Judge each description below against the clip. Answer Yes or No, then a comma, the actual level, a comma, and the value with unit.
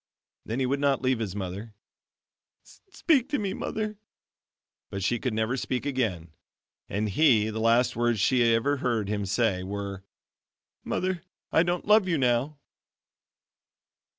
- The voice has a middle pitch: No, low, 120 Hz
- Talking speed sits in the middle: Yes, average, 150 wpm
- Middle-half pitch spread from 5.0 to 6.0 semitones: Yes, average, 5.3 semitones